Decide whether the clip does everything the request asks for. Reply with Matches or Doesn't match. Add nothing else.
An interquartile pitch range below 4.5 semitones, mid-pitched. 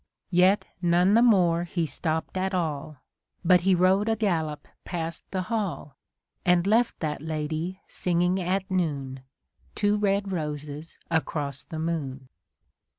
Matches